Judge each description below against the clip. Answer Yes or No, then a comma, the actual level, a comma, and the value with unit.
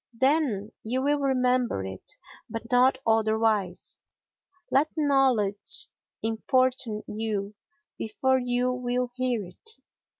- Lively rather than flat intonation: No, average, 3.1 semitones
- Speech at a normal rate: No, slow, 100 wpm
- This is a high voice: Yes, high, 245 Hz